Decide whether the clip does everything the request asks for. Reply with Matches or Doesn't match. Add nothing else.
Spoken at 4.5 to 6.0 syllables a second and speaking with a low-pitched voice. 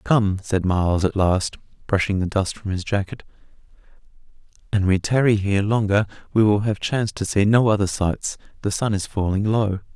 Matches